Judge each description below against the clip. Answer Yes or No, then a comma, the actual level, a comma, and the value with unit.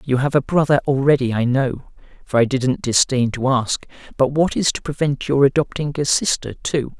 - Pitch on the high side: No, low, 135 Hz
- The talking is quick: No, average, 195 wpm